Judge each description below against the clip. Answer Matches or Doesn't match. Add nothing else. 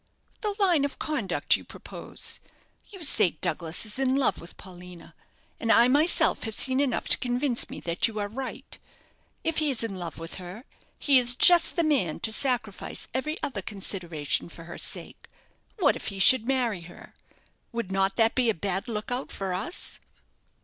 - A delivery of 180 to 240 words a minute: Matches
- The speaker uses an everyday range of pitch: Doesn't match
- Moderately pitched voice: Doesn't match